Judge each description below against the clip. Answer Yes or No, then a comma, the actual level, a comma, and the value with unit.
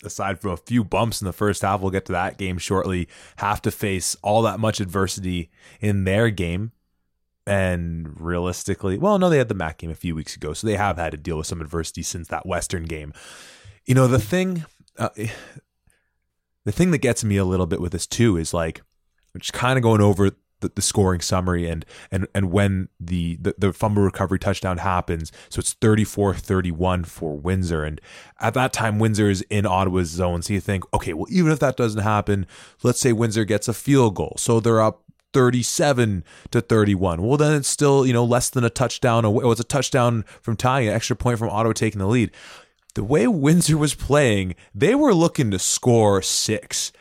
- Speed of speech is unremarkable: No, fast, 210 wpm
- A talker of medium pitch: No, low, 100 Hz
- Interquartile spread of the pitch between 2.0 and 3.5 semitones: No, average, 4.6 semitones